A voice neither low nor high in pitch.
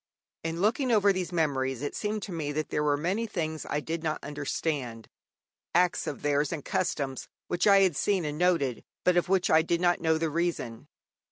Yes: medium, 165 Hz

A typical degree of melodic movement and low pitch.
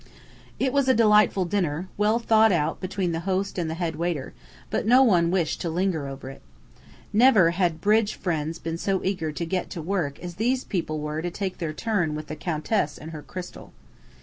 No: average, 4.2 semitones; medium, 175 Hz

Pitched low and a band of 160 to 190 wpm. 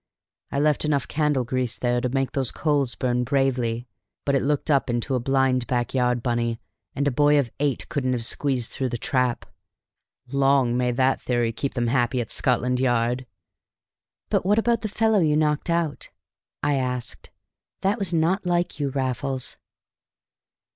Yes: low, 130 Hz; average, 170 wpm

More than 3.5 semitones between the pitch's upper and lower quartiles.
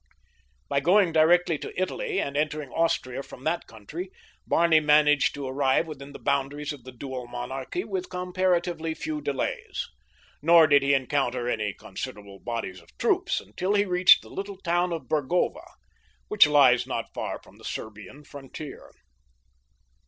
Yes: average, 4.7 semitones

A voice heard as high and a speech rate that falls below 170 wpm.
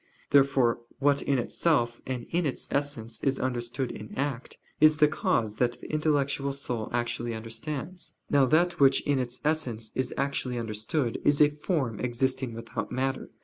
No: low, 130 Hz; average, 160 wpm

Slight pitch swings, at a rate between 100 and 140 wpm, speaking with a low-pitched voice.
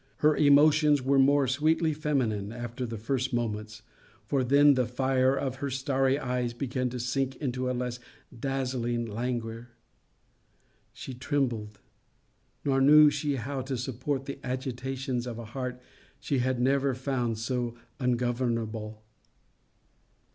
Yes: narrow, 2.3 semitones; slow, 135 wpm; low, 130 Hz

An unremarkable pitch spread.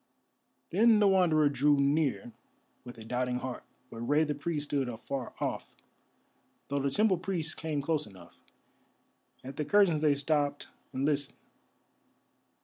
Yes: average, 3.1 semitones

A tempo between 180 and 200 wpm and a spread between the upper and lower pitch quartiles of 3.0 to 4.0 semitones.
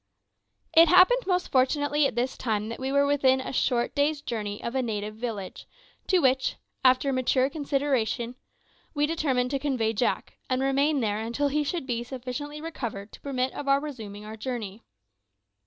No: average, 170 wpm; average, 3.6 semitones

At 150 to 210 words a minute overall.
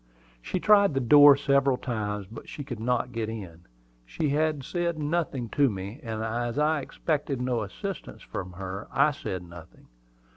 Yes: average, 160 wpm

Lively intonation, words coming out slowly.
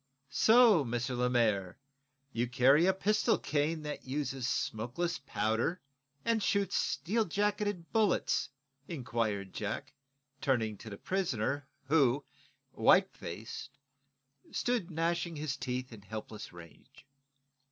Yes: wide, 6.9 semitones; slow, 110 wpm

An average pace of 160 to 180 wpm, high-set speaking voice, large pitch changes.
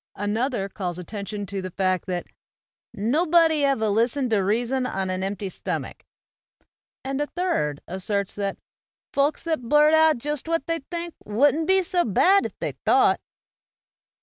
No: average, 150 wpm; high, 235 Hz; wide, 7.8 semitones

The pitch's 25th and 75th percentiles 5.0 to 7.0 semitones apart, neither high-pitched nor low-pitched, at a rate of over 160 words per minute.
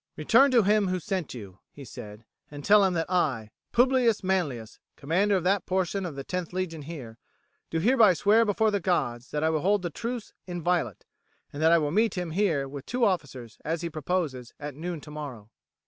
Yes: wide, 5.6 semitones; medium, 170 Hz; average, 200 wpm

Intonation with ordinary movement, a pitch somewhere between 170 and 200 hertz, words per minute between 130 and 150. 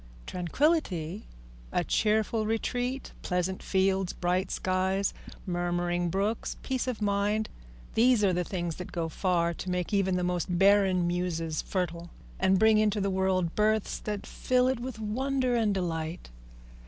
Yes: average, 3.5 semitones; high, 190 Hz; average, 145 wpm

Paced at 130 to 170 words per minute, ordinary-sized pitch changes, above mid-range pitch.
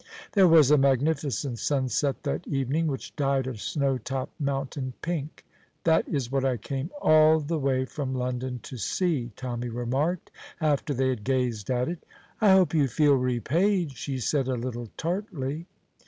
No: average, 165 wpm; average, 3.5 semitones; low, 135 Hz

